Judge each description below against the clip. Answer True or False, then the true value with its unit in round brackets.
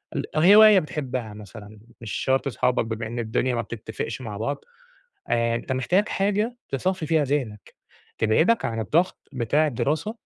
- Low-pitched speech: True (130 Hz)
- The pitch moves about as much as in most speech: False (6.0 semitones)